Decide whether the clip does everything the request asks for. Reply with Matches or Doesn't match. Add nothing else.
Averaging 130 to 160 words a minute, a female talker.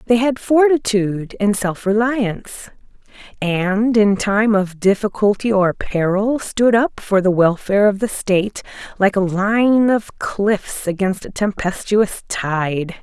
Matches